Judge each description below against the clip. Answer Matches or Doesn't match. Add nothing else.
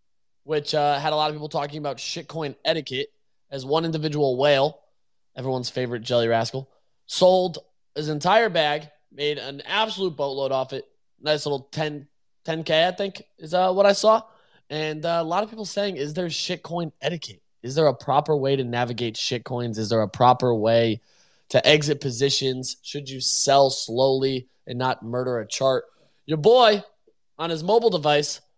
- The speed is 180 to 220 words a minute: Doesn't match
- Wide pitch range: Doesn't match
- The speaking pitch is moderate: Matches